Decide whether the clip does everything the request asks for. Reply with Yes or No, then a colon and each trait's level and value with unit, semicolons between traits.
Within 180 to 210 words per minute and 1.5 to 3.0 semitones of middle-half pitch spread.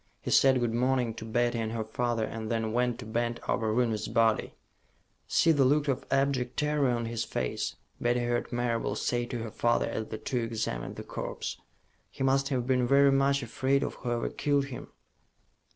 Yes: average, 190 wpm; narrow, 2.6 semitones